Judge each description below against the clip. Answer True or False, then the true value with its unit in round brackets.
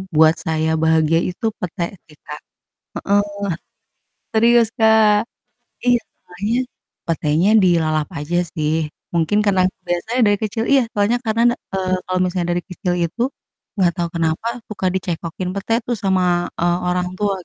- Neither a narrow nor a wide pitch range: True (4.0 semitones)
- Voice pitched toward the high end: False (180 Hz)